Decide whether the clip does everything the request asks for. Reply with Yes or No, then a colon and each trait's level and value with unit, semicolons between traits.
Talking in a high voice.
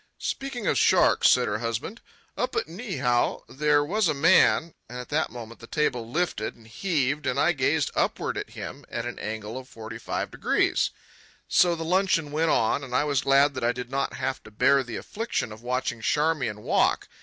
No: medium, 140 Hz